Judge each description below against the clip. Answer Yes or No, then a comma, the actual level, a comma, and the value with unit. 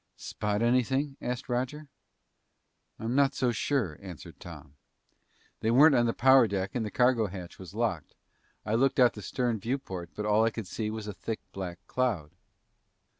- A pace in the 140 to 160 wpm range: No, average, 175 wpm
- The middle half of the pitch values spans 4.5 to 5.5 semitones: No, average, 4.0 semitones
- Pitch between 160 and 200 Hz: No, low, 115 Hz